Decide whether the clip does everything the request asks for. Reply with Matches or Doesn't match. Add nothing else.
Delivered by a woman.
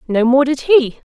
Matches